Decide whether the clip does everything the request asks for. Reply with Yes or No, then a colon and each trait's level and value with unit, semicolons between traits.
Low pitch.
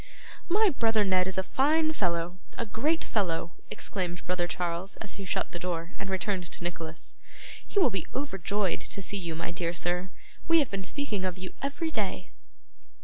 No: high, 190 Hz